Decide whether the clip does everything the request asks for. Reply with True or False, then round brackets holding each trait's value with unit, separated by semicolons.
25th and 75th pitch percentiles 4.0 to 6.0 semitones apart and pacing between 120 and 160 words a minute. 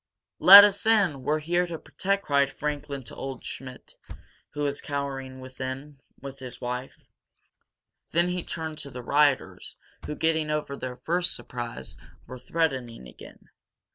False (3.6 semitones; 150 wpm)